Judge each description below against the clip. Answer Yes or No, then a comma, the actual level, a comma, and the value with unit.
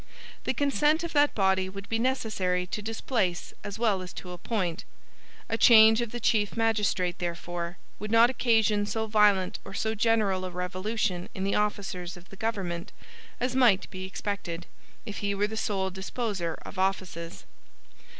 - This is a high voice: Yes, high, 200 Hz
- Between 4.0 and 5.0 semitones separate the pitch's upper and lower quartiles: No, average, 3.3 semitones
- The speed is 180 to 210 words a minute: No, average, 165 wpm